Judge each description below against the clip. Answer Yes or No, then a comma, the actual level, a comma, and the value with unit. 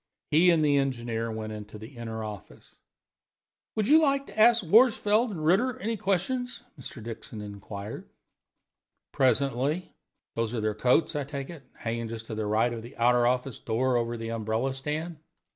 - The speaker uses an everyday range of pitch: No, wide, 7.2 semitones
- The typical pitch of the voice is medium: No, low, 125 Hz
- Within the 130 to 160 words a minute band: No, average, 170 wpm